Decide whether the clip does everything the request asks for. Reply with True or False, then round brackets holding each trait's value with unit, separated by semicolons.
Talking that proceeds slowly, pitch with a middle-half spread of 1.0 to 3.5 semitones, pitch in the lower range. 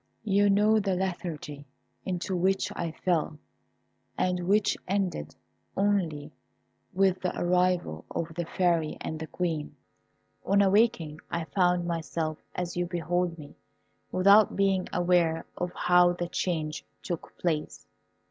False (130 wpm; 2.6 semitones; 175 Hz)